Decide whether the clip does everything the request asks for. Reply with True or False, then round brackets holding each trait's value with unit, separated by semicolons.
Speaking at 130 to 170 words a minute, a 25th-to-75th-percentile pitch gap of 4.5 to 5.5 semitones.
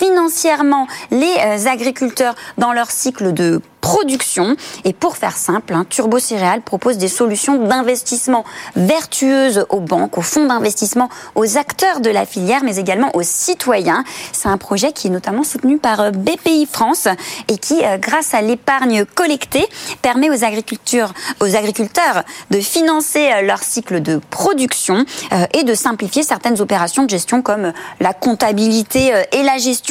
True (145 wpm; 4.8 semitones)